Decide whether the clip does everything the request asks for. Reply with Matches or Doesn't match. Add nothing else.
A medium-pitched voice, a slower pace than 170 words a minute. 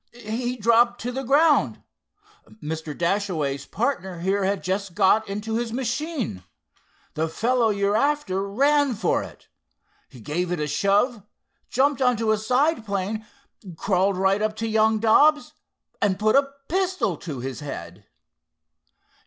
Doesn't match